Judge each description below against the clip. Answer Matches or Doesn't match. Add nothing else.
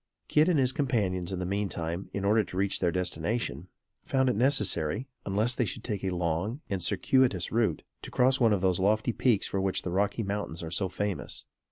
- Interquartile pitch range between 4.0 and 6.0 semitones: Matches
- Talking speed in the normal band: Doesn't match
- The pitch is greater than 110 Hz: Doesn't match